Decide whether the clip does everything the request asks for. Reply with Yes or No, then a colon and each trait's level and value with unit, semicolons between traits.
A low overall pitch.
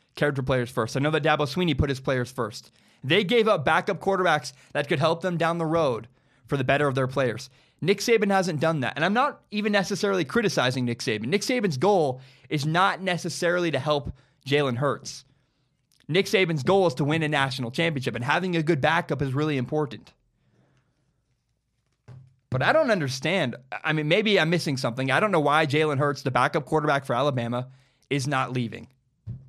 No: medium, 145 Hz